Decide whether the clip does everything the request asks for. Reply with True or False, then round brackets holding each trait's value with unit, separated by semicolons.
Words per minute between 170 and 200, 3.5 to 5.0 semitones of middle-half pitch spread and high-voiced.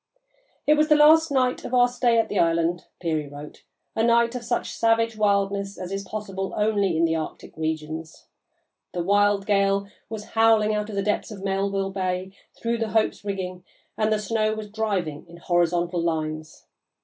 True (180 wpm; 4.1 semitones; 200 Hz)